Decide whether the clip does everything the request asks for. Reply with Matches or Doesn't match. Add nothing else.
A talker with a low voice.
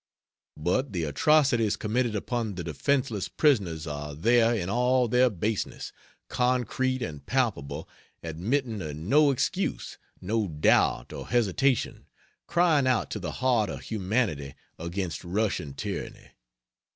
Matches